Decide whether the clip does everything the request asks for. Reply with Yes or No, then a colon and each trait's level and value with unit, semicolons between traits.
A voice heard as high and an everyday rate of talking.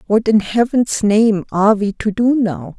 Yes: high, 215 Hz; average, 195 wpm